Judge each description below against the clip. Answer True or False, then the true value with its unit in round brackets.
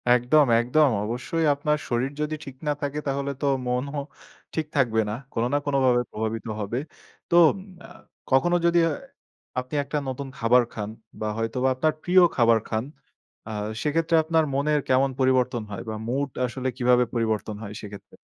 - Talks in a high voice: False (130 Hz)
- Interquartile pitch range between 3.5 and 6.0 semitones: True (3.9 semitones)